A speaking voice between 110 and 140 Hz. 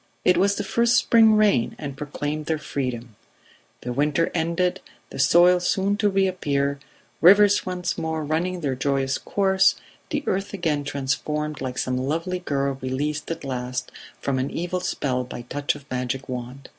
No: medium, 150 Hz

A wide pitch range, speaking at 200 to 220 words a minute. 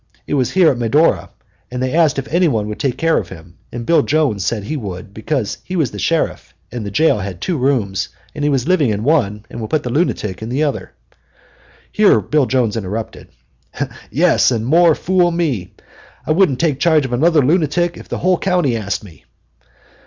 Yes: wide, 6.9 semitones; fast, 205 wpm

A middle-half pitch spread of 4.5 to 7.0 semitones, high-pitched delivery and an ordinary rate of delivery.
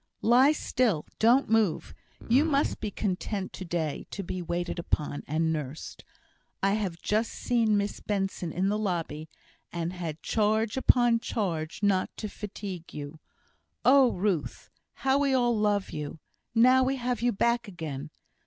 Yes: wide, 5.6 semitones; high, 205 Hz; average, 155 wpm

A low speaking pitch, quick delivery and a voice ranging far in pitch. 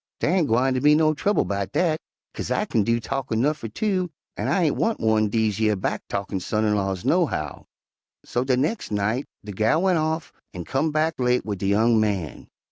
Yes: low, 115 Hz; fast, 210 wpm; wide, 6.7 semitones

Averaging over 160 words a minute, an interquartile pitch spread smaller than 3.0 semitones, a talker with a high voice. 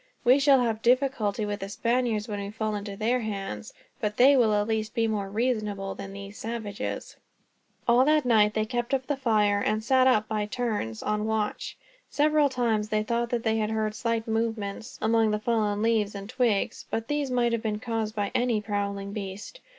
Yes: average, 190 wpm; narrow, 2.4 semitones; high, 220 Hz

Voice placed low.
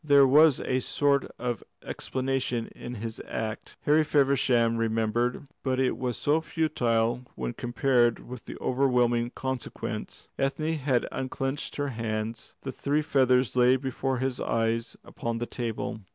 Yes: low, 125 Hz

